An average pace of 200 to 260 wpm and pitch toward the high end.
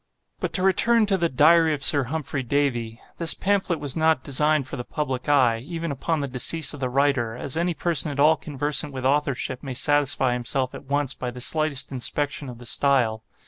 No: fast, 205 wpm; medium, 140 Hz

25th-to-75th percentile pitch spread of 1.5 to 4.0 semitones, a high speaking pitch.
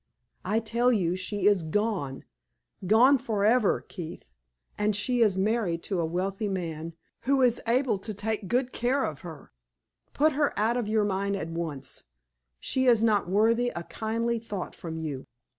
No: average, 4.8 semitones; high, 210 Hz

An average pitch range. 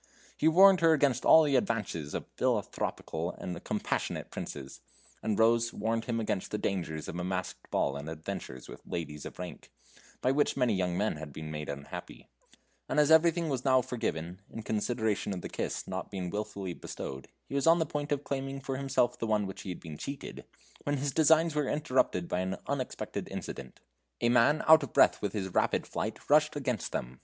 No: wide, 7.9 semitones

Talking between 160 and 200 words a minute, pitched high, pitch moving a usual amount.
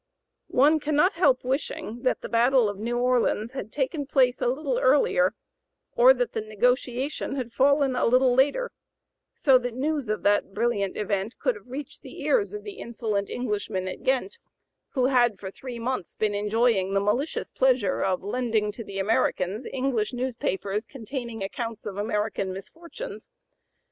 Yes: average, 165 wpm; high, 245 Hz; average, 4.2 semitones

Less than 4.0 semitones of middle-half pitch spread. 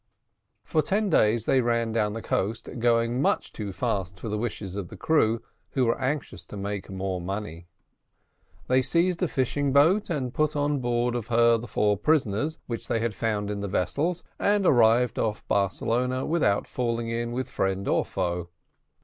No: average, 4.4 semitones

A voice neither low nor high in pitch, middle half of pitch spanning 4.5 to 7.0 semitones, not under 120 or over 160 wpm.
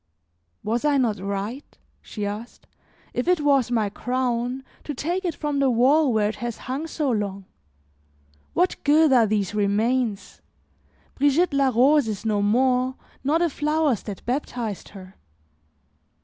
No: very high, 250 Hz; average, 5.1 semitones; average, 150 wpm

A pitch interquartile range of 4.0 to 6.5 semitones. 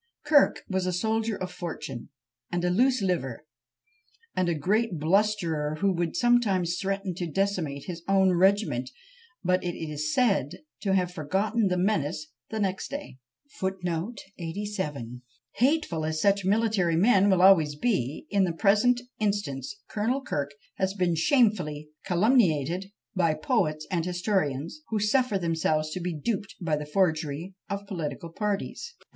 Yes: average, 4.5 semitones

